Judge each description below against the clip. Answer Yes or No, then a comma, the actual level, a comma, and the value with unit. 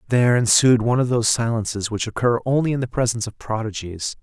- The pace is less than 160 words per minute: No, average, 200 wpm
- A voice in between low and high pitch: No, low, 115 Hz